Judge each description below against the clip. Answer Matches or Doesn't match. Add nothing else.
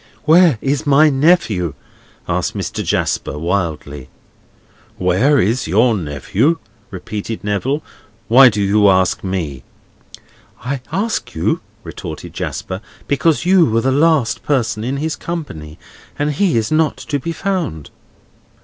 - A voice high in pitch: Doesn't match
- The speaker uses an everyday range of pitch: Doesn't match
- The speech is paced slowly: Matches